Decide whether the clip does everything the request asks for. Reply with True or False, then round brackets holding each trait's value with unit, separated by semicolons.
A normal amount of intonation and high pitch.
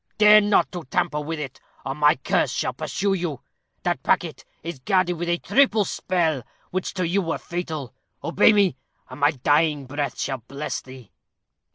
False (4.6 semitones; 165 Hz)